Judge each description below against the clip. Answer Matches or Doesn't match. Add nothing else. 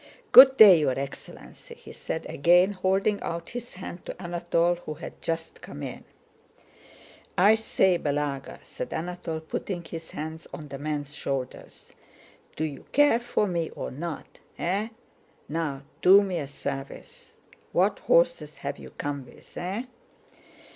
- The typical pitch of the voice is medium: Matches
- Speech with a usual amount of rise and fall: Matches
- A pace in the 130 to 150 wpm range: Matches